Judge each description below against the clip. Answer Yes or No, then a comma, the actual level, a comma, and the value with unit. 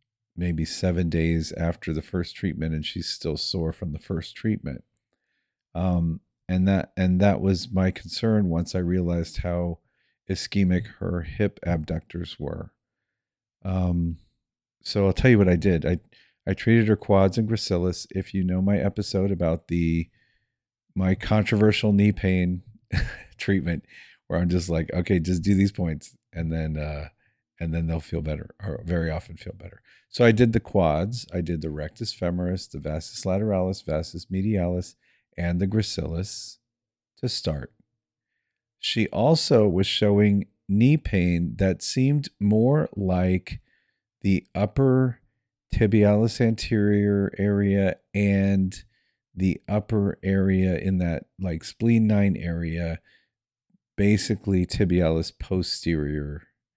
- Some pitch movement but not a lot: Yes, average, 3.4 semitones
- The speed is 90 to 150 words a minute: Yes, slow, 135 wpm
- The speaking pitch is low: Yes, very low, 95 Hz